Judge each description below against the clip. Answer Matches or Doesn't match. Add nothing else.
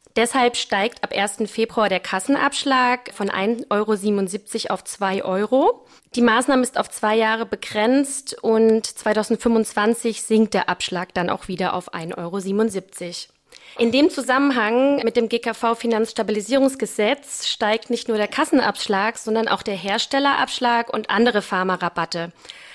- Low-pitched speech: Doesn't match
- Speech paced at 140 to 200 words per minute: Doesn't match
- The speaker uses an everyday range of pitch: Matches